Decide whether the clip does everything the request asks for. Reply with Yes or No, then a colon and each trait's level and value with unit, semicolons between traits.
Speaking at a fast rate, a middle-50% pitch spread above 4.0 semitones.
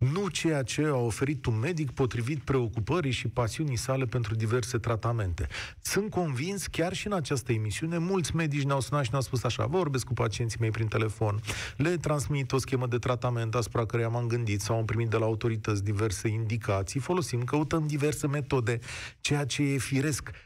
Yes: fast, 180 wpm; average, 4.4 semitones